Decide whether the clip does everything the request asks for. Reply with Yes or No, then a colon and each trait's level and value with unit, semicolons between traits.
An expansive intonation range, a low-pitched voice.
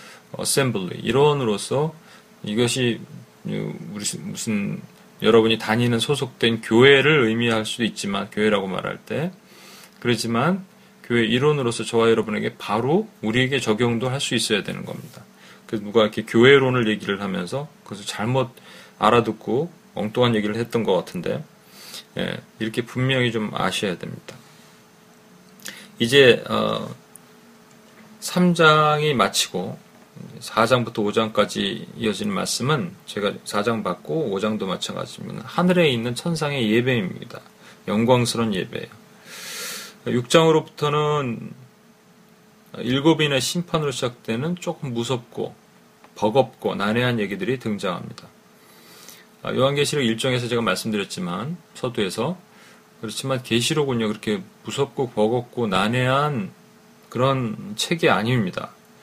Yes: wide, 7.0 semitones; low, 130 Hz